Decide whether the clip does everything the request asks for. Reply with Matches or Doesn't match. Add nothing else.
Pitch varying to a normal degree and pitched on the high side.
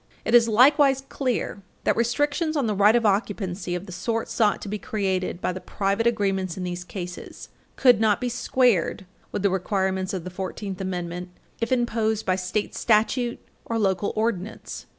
Matches